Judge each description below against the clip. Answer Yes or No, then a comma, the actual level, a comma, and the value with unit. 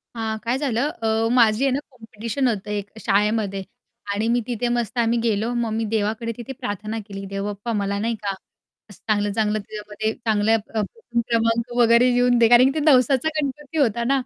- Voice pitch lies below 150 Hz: No, high, 225 Hz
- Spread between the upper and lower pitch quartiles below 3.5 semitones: Yes, narrow, 2.5 semitones